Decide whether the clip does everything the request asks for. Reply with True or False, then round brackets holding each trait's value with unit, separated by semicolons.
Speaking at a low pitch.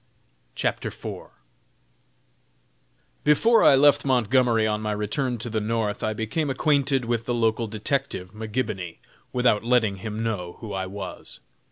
True (115 Hz)